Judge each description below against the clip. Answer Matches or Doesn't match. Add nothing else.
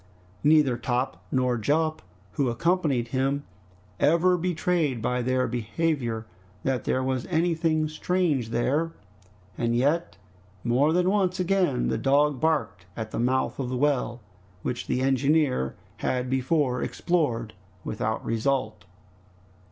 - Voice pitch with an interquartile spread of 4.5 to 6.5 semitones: Matches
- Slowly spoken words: Matches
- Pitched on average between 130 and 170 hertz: Matches